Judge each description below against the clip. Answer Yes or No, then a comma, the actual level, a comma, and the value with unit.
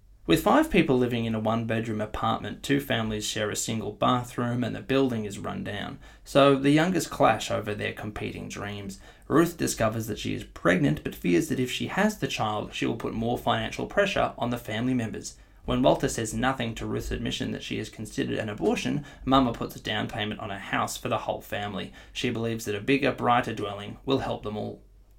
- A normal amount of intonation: Yes, average, 3.7 semitones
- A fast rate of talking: Yes, fast, 210 wpm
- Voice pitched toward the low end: Yes, low, 115 Hz